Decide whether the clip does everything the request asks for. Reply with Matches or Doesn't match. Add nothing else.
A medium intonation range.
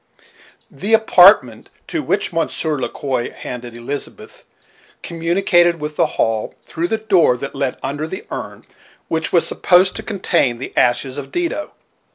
Doesn't match